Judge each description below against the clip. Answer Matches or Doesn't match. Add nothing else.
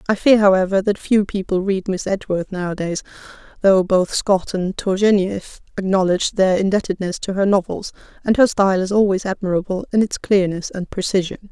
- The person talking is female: Matches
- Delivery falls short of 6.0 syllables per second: Matches